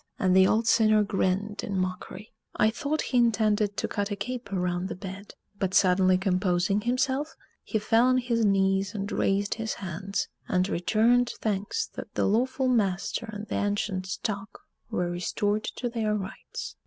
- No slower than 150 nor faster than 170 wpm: Yes, average, 165 wpm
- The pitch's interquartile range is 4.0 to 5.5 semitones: No, average, 3.0 semitones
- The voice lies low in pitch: No, high, 205 Hz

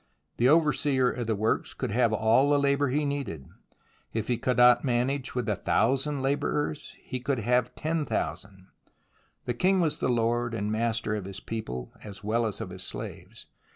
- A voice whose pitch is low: Yes, low, 120 Hz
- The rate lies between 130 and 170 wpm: No, average, 190 wpm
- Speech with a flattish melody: No, average, 4.2 semitones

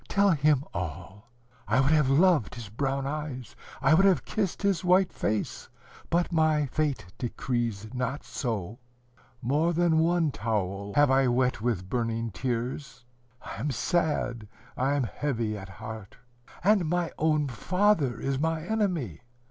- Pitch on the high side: No, low, 135 Hz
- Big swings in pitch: Yes, wide, 5.7 semitones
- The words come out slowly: No, average, 150 wpm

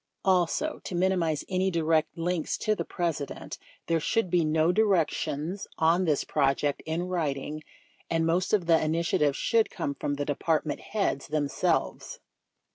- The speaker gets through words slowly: No, average, 150 wpm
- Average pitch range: Yes, average, 3.0 semitones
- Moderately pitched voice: Yes, medium, 165 Hz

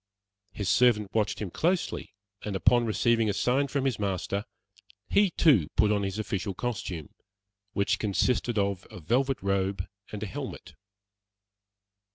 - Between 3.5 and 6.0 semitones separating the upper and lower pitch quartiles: Yes, average, 3.8 semitones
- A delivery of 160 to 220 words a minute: No, average, 145 wpm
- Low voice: Yes, low, 105 Hz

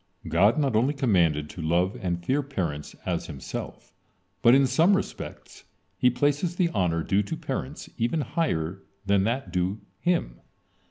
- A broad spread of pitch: Yes, wide, 8.1 semitones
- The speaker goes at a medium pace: Yes, average, 155 wpm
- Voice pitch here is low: Yes, low, 105 Hz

